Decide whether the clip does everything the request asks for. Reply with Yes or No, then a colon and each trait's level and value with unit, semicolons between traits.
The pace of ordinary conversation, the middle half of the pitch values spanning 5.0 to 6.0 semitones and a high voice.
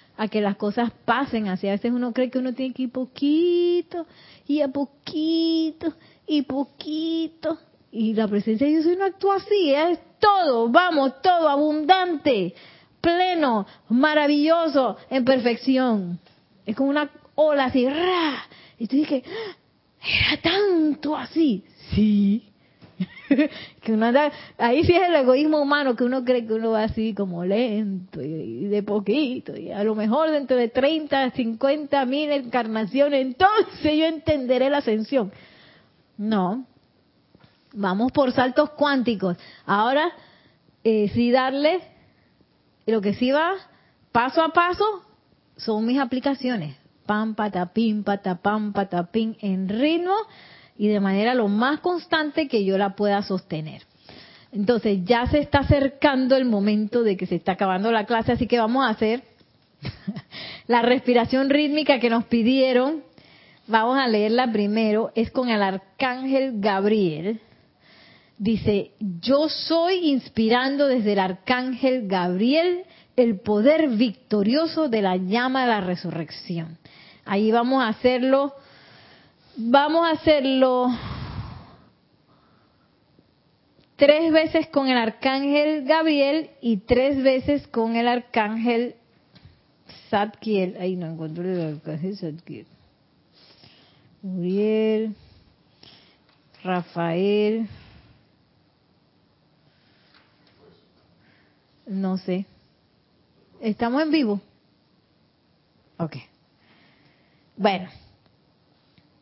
No: slow, 115 wpm; wide, 5.6 semitones; high, 245 Hz